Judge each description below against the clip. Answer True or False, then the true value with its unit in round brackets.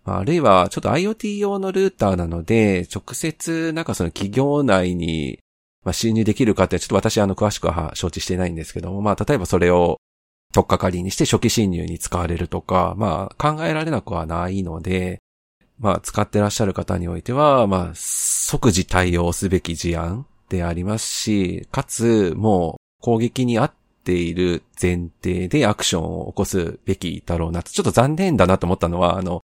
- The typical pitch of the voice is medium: False (95 Hz)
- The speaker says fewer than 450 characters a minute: True (370 characters per minute)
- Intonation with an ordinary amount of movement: True (4.4 semitones)